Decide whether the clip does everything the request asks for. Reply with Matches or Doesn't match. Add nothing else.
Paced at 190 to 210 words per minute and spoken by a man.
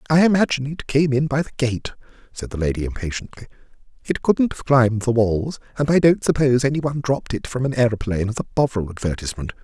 Matches